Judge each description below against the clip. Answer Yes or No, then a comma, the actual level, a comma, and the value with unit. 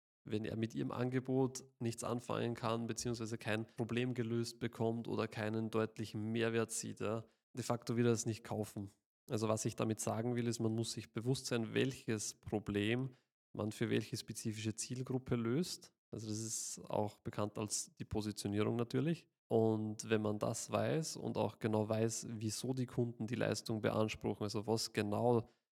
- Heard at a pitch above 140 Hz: No, low, 115 Hz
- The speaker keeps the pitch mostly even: Yes, narrow, 1.9 semitones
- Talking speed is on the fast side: No, average, 170 wpm